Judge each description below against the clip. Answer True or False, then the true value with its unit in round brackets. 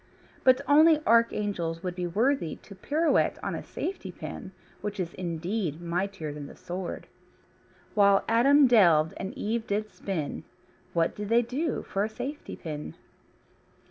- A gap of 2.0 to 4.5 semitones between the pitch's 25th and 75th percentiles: False (5.5 semitones)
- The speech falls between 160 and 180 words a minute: False (145 wpm)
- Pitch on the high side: True (200 Hz)